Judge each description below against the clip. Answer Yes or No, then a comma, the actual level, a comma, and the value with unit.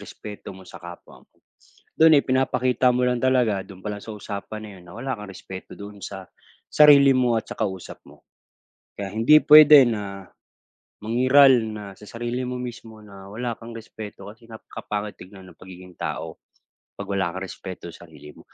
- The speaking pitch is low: Yes, low, 105 Hz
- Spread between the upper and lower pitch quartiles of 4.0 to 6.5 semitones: Yes, average, 4.3 semitones